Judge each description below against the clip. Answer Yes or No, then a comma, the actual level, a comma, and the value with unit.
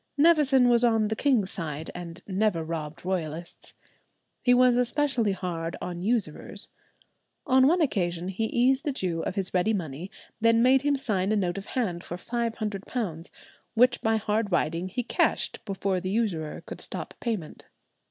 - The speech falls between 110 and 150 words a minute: No, average, 170 wpm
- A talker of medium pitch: No, high, 205 Hz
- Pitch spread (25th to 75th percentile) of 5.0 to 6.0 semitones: Yes, wide, 5.6 semitones